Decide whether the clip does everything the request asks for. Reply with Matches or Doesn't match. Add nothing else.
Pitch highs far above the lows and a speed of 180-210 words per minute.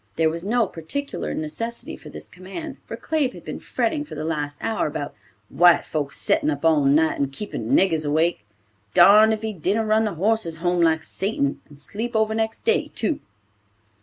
Matches